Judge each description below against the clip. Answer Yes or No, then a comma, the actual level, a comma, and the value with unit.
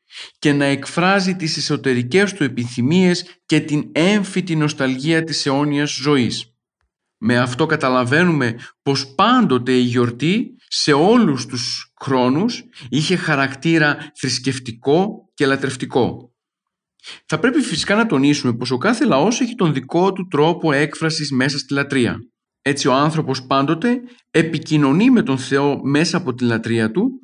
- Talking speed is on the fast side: No, average, 135 wpm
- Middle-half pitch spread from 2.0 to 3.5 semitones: No, average, 5.0 semitones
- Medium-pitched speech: Yes, medium, 145 Hz